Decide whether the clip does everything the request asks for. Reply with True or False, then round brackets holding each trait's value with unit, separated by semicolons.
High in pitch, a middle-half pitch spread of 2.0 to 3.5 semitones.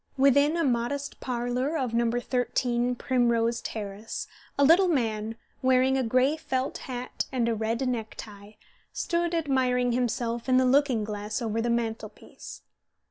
True (245 Hz; 2.5 semitones)